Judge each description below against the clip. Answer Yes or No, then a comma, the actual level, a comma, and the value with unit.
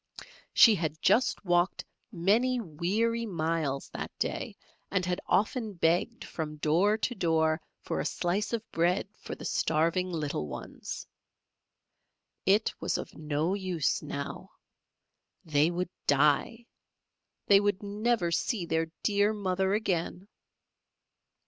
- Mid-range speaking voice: Yes, medium, 180 Hz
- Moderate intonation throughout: Yes, average, 4.3 semitones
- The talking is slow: Yes, slow, 125 wpm